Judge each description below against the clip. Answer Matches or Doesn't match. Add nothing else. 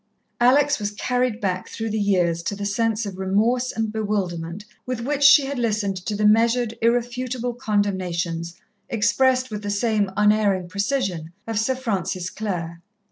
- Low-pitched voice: Doesn't match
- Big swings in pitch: Doesn't match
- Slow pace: Doesn't match